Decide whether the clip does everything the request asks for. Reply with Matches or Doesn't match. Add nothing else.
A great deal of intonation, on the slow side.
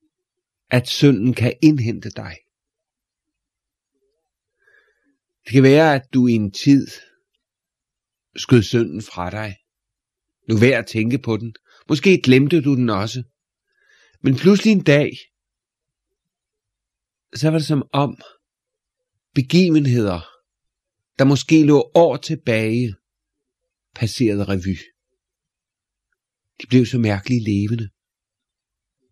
Matches